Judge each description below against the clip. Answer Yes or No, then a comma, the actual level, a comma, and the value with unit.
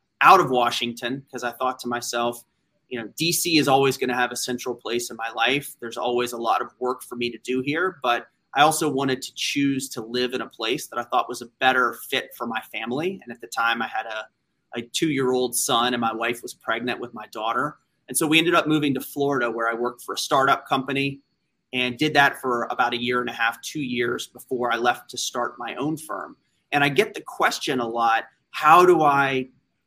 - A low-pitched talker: Yes, low, 125 Hz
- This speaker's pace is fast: Yes, fast, 240 wpm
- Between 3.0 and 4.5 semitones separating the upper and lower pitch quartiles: No, narrow, 2.6 semitones